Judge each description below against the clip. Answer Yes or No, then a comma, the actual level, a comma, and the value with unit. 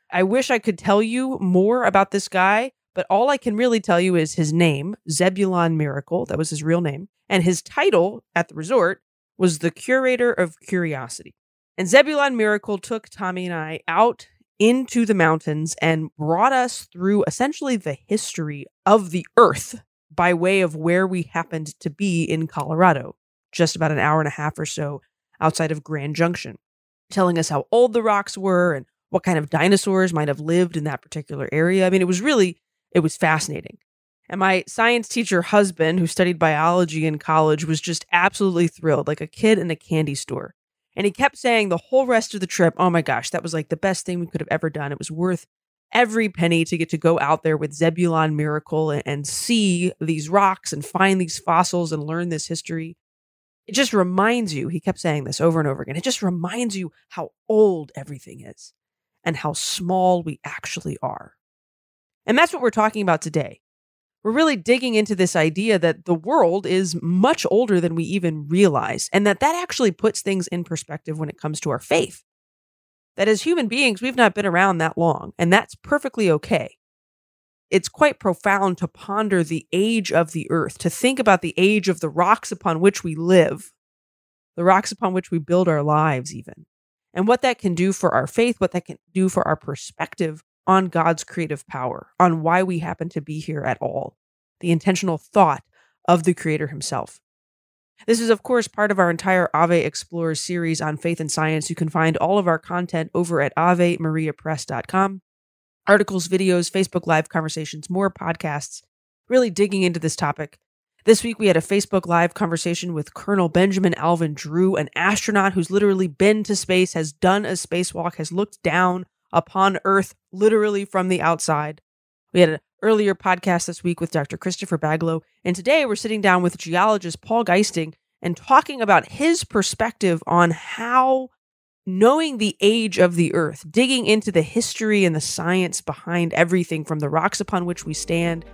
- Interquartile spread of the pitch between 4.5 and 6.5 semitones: No, average, 3.7 semitones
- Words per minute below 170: No, average, 190 wpm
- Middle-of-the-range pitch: Yes, medium, 175 Hz